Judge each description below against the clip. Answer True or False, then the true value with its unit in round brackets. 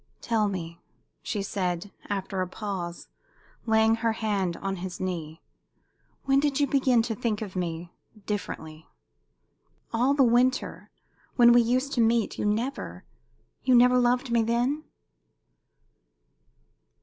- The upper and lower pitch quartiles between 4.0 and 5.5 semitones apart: True (4.6 semitones)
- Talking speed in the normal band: False (130 wpm)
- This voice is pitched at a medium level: False (225 Hz)